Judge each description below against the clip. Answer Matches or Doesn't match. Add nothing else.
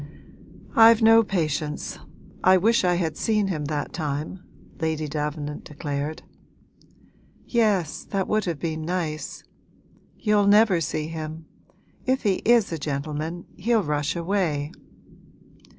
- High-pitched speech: Doesn't match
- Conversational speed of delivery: Doesn't match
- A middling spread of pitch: Matches